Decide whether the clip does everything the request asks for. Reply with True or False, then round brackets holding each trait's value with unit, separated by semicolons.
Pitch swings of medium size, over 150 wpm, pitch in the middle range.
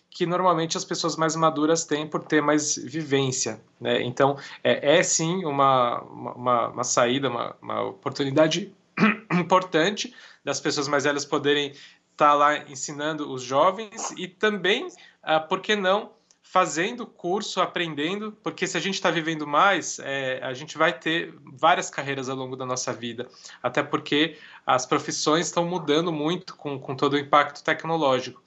True (3.7 semitones; 160 wpm; 155 Hz)